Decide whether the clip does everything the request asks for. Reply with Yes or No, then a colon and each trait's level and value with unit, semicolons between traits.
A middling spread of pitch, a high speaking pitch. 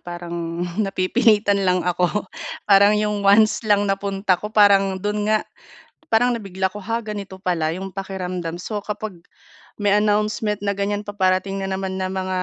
No: narrow, 1.9 semitones; high, 195 Hz